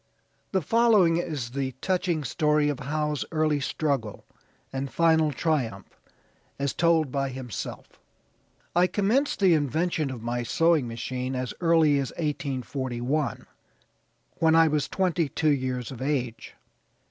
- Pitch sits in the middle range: Yes, medium, 150 Hz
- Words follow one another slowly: Yes, slow, 130 wpm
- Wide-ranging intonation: No, average, 4.0 semitones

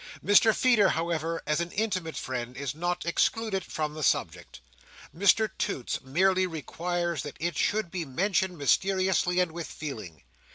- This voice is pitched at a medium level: Yes, medium, 170 Hz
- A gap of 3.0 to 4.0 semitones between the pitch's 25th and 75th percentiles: Yes, average, 3.7 semitones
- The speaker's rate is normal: Yes, average, 150 wpm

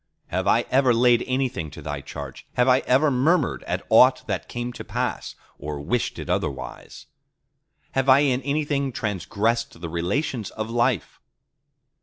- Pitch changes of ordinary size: No, wide, 6.0 semitones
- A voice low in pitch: Yes, low, 120 Hz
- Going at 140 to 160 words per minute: Yes, average, 155 wpm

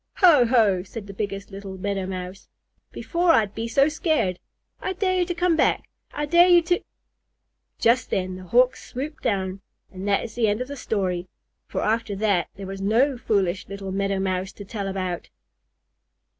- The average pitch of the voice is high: Yes, high, 205 Hz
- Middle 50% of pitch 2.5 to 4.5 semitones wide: No, wide, 5.5 semitones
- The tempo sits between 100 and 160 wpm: No, average, 185 wpm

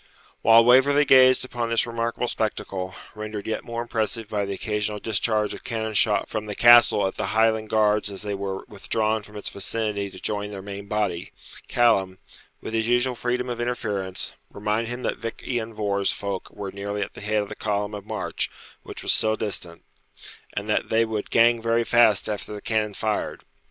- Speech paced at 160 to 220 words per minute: Yes, average, 190 wpm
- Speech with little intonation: Yes, narrow, 2.2 semitones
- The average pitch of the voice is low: Yes, low, 110 Hz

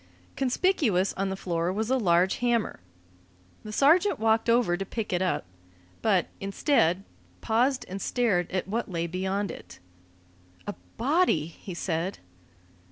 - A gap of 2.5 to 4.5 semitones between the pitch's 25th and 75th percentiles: No, average, 4.9 semitones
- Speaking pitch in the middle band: No, high, 195 Hz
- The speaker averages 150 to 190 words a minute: No, average, 140 wpm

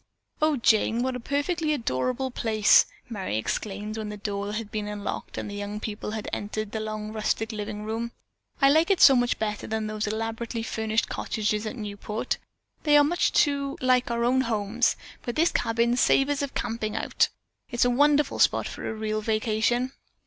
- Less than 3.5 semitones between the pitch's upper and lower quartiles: Yes, average, 3.0 semitones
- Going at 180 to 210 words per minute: Yes, average, 185 wpm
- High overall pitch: Yes, high, 225 Hz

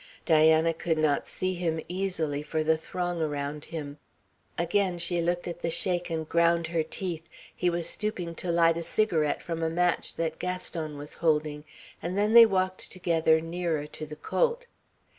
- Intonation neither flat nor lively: No, narrow, 2.0 semitones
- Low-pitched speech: No, medium, 165 Hz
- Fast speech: No, average, 175 wpm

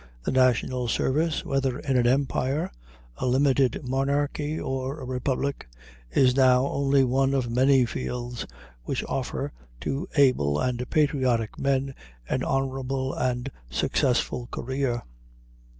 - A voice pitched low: Yes, low, 130 Hz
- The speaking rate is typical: No, slow, 120 wpm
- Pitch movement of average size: No, narrow, 1.6 semitones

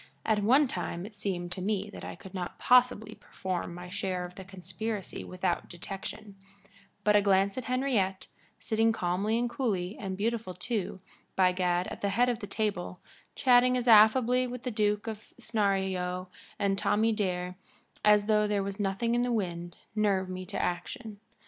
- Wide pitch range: No, average, 3.3 semitones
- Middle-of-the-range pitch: No, high, 200 Hz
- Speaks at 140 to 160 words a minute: No, average, 175 wpm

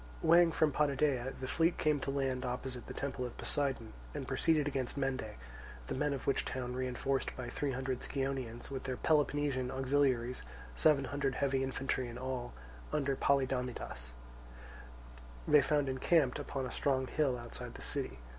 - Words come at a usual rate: Yes, average, 160 wpm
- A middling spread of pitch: No, narrow, 2.0 semitones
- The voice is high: No, low, 135 Hz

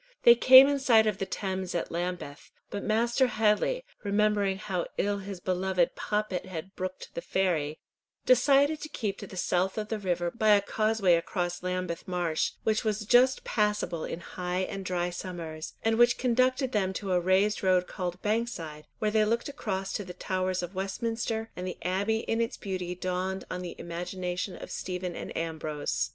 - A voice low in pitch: No, high, 190 Hz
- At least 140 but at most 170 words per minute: No, average, 180 wpm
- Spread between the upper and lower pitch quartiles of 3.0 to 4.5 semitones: Yes, average, 3.3 semitones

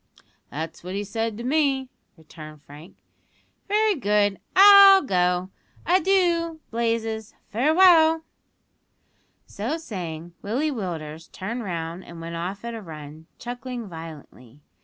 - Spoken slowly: Yes, slow, 115 wpm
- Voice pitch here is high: Yes, high, 210 Hz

